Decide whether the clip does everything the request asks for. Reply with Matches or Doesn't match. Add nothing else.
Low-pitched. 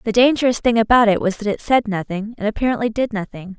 Doesn't match